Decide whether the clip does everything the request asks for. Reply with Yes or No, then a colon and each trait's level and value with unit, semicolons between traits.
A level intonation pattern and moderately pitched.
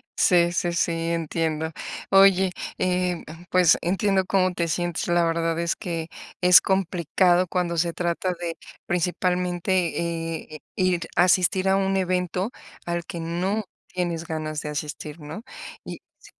Yes: narrow, 1.7 semitones; medium, 175 Hz